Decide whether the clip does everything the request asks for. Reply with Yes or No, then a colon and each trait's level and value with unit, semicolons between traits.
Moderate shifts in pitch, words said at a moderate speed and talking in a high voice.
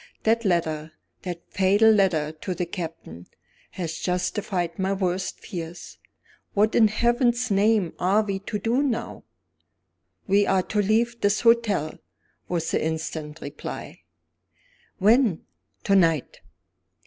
No: average, 4.5 semitones; slow, 125 wpm; high, 195 Hz